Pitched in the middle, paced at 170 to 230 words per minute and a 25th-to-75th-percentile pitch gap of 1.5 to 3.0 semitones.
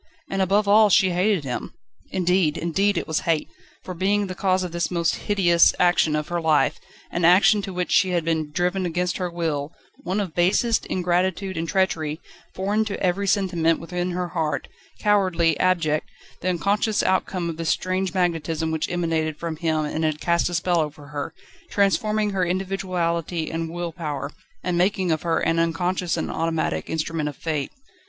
Yes: medium, 175 Hz; average, 180 wpm; narrow, 2.5 semitones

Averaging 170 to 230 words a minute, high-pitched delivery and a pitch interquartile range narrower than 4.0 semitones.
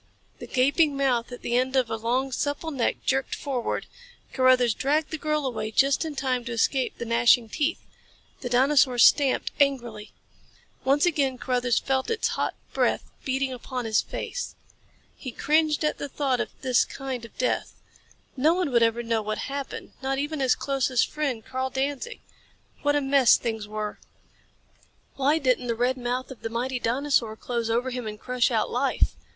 Yes: average, 180 wpm; very high, 260 Hz; average, 2.7 semitones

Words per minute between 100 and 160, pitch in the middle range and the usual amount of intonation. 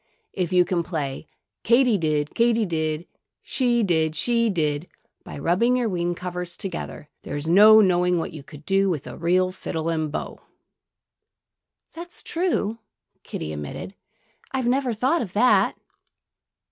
No: average, 145 wpm; medium, 180 Hz; wide, 6.4 semitones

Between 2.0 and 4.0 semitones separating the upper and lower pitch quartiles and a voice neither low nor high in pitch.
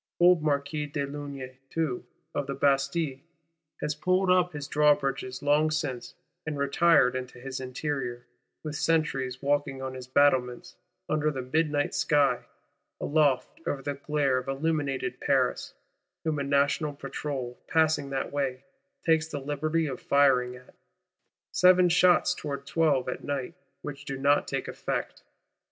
Yes: narrow, 2.5 semitones; medium, 145 Hz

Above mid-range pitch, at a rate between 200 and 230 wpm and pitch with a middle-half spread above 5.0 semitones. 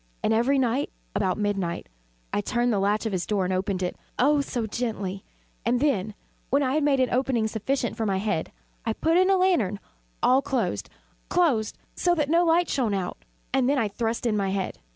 Yes: high, 230 Hz; fast, 205 wpm; wide, 5.4 semitones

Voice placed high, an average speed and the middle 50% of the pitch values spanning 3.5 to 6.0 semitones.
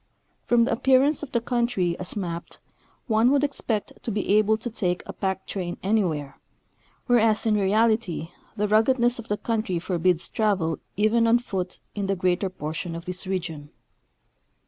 Yes: high, 210 Hz; average, 165 wpm; average, 4.2 semitones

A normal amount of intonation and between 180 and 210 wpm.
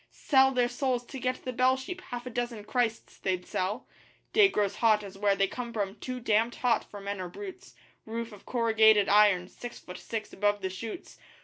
Yes: average, 3.6 semitones; fast, 205 wpm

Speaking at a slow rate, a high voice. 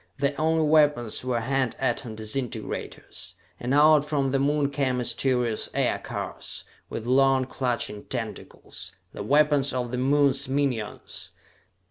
No: slow, 125 wpm; low, 135 Hz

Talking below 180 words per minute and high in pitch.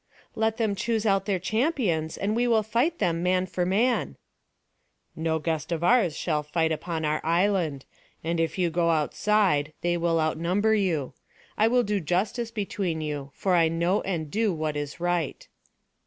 No: average, 170 wpm; medium, 175 Hz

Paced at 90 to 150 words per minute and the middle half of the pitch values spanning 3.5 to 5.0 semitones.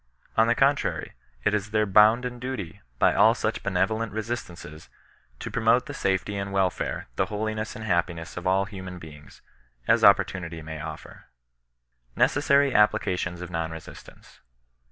Yes: average, 145 wpm; average, 4.1 semitones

